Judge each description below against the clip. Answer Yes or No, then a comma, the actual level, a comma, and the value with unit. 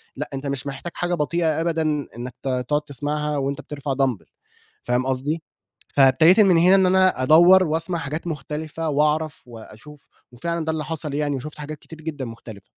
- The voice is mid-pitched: Yes, medium, 150 Hz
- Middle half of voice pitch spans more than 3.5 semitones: No, average, 3.0 semitones